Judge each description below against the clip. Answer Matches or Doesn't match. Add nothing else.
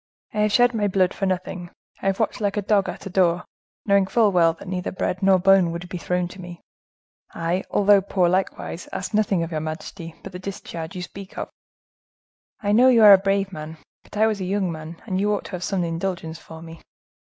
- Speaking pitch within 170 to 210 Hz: Matches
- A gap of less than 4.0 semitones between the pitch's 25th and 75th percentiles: Matches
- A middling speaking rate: Doesn't match